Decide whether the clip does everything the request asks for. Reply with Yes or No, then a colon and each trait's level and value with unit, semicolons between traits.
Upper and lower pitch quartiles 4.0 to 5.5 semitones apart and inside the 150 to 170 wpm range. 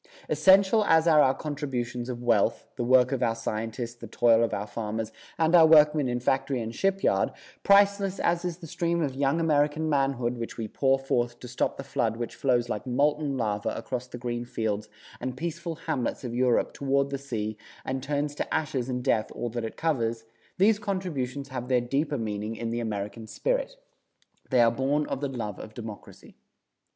No: average, 4.3 semitones; average, 190 wpm